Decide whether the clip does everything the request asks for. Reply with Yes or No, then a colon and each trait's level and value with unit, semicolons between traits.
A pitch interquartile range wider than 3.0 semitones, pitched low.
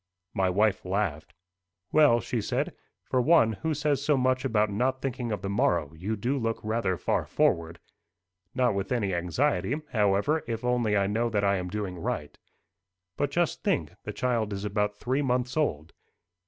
Yes: average, 4.6 semitones; low, 110 Hz